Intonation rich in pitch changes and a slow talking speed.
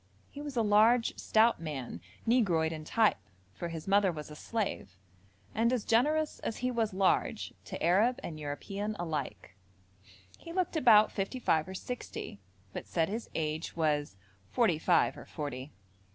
No: wide, 6.7 semitones; average, 160 wpm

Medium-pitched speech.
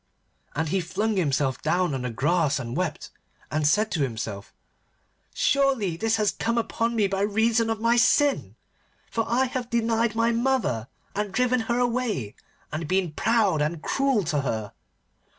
No: high, 205 Hz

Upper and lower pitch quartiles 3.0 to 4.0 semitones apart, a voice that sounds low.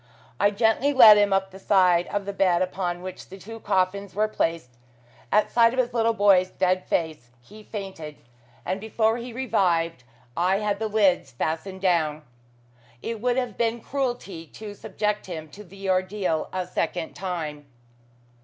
No: average, 3.5 semitones; high, 195 Hz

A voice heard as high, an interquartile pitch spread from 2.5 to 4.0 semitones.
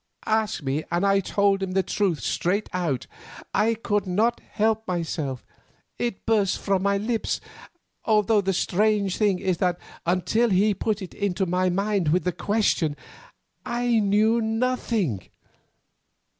Yes: high, 200 Hz; average, 3.2 semitones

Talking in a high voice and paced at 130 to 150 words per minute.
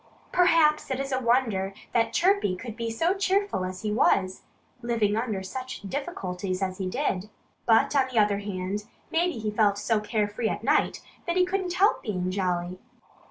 No: high, 225 Hz; average, 175 wpm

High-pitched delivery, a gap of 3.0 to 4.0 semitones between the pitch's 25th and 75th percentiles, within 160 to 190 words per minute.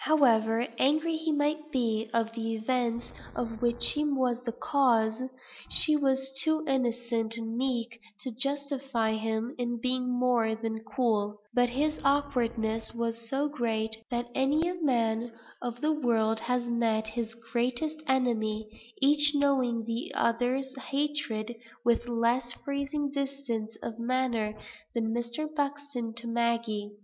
No: high, 240 Hz; average, 3.3 semitones; average, 140 wpm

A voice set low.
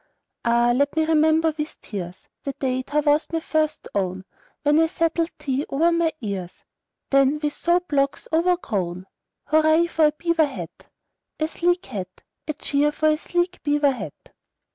No: very high, 300 Hz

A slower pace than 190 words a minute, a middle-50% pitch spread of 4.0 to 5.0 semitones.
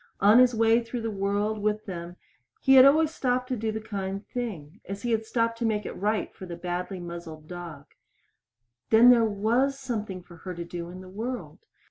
No: average, 200 wpm; average, 4.5 semitones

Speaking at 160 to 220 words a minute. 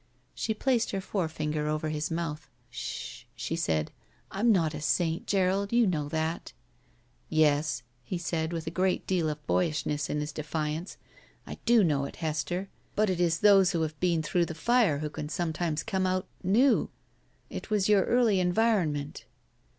Yes: average, 180 wpm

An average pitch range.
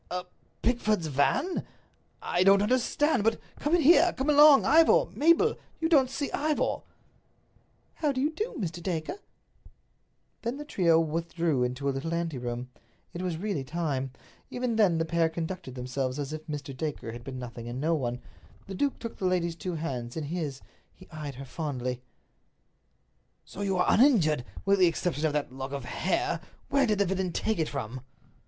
No: wide, 8.7 semitones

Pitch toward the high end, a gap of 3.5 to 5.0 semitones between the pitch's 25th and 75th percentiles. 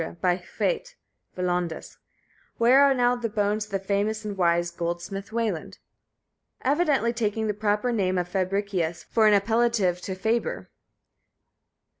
Yes: high, 205 Hz; average, 4.1 semitones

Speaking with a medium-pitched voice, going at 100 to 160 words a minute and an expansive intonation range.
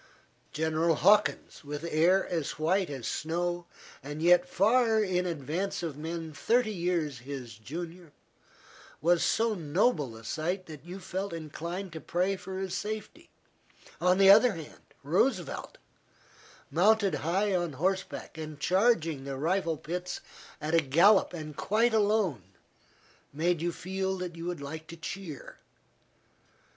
No: medium, 175 Hz; average, 140 wpm; average, 3.7 semitones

